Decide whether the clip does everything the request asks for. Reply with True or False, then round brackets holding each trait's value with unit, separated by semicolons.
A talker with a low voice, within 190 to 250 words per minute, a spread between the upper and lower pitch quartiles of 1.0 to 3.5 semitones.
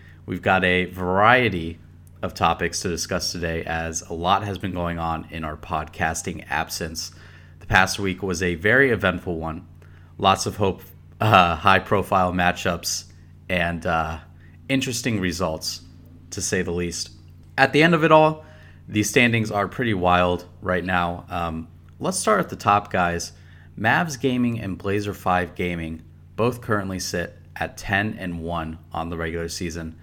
False (90 Hz; 160 wpm; 2.5 semitones)